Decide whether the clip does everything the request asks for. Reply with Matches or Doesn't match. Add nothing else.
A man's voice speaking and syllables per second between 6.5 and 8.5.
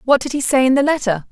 Doesn't match